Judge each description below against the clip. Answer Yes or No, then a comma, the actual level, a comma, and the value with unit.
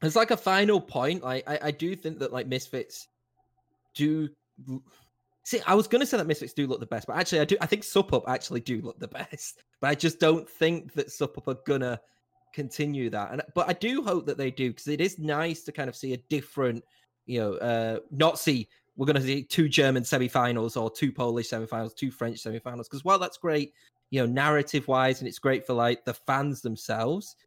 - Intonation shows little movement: No, average, 4.2 semitones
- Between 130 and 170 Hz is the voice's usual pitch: Yes, medium, 140 Hz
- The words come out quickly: Yes, fast, 225 wpm